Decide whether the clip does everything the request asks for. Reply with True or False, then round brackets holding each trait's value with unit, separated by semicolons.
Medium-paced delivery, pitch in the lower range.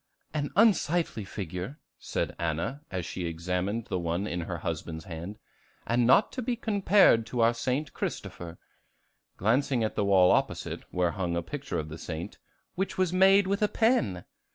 True (170 wpm; 105 Hz)